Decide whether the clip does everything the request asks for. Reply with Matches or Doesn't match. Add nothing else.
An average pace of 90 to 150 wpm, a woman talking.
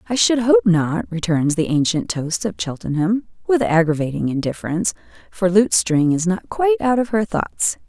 Doesn't match